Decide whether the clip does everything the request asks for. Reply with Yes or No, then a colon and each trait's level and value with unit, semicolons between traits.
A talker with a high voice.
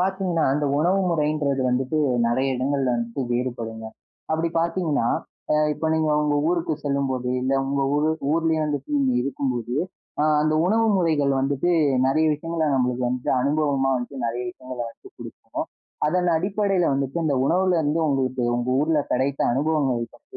No: medium, 145 Hz